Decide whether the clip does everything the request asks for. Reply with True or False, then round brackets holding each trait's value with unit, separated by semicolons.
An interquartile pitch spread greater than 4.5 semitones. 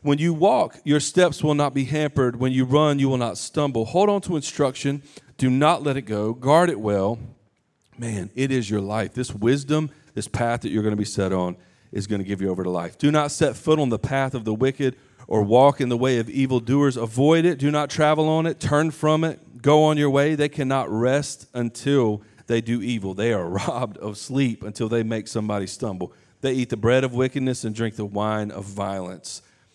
True (5.0 semitones)